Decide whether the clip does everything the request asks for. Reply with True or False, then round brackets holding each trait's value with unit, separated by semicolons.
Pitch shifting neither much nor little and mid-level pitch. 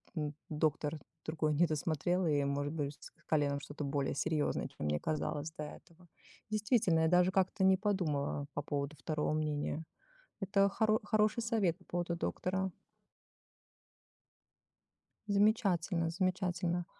True (4.2 semitones; 165 Hz)